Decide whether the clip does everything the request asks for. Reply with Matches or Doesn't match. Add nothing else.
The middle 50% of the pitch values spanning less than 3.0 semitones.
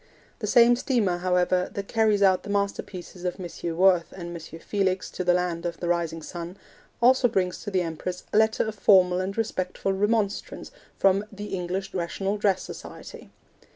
Matches